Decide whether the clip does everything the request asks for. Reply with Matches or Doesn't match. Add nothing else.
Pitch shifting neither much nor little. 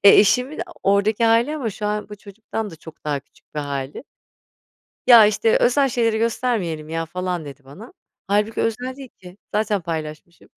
Doesn't match